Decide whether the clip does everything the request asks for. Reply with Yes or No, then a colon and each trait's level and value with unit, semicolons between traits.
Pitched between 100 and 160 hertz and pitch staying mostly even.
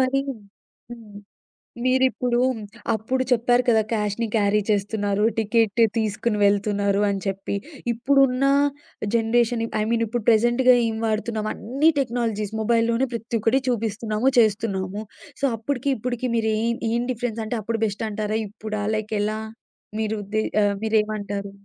No: high, 220 Hz; narrow, 2.2 semitones